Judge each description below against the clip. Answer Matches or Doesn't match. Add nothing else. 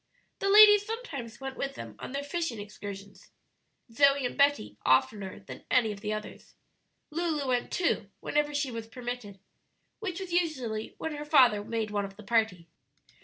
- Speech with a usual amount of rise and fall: Doesn't match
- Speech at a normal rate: Matches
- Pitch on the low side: Doesn't match